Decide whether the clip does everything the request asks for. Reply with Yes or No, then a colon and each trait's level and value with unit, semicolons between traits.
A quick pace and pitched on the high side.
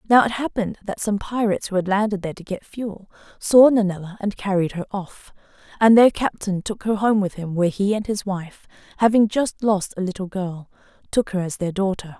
Yes: fast, 210 wpm; high, 200 Hz